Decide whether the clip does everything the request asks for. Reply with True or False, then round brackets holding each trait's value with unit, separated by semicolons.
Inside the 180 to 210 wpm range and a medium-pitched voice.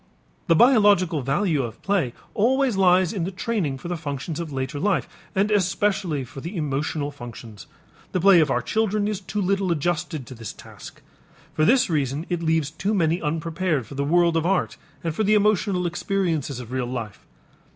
True (185 wpm; 170 Hz)